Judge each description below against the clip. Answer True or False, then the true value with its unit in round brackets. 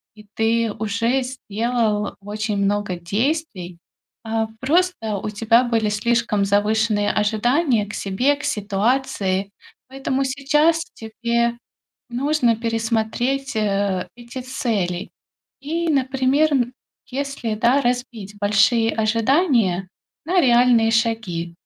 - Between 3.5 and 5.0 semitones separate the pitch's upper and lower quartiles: True (3.9 semitones)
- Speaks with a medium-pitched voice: False (230 Hz)